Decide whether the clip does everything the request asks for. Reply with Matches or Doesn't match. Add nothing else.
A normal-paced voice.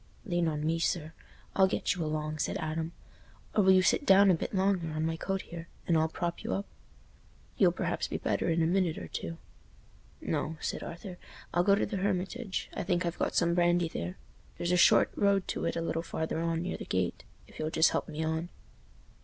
Doesn't match